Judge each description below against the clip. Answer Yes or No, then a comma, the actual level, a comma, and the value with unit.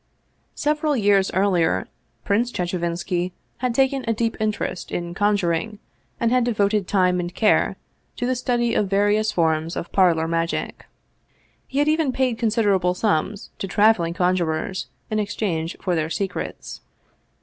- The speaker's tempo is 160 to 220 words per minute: No, average, 145 wpm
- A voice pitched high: Yes, high, 200 Hz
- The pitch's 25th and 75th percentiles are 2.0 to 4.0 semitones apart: No, average, 4.6 semitones